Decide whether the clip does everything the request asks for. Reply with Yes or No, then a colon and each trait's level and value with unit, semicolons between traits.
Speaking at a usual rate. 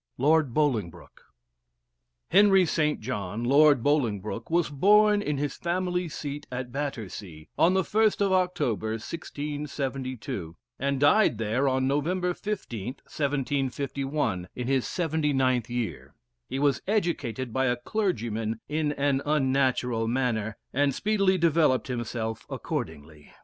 No: slow, 120 wpm